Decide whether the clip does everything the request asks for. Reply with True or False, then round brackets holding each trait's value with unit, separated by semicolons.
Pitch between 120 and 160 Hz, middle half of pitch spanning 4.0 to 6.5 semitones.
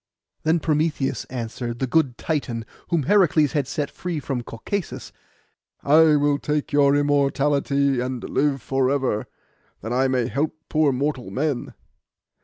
False (140 Hz; 2.8 semitones)